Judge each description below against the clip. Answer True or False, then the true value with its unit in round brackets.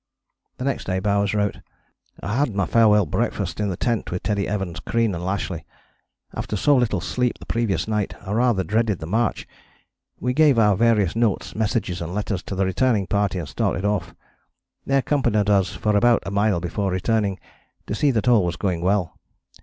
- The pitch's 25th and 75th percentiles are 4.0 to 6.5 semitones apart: False (3.4 semitones)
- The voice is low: True (105 Hz)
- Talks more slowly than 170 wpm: False (190 wpm)